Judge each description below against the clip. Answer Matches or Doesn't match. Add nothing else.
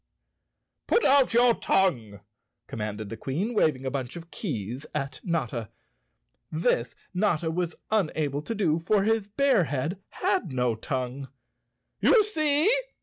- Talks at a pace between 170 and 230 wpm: Doesn't match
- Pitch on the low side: Doesn't match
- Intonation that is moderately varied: Doesn't match